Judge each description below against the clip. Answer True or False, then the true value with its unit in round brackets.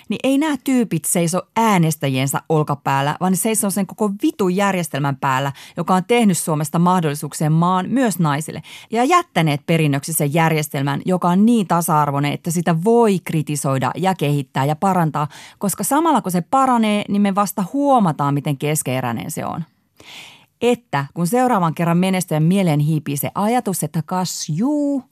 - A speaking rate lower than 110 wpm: False (155 wpm)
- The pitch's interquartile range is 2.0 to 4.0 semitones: False (5.4 semitones)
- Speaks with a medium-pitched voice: True (175 Hz)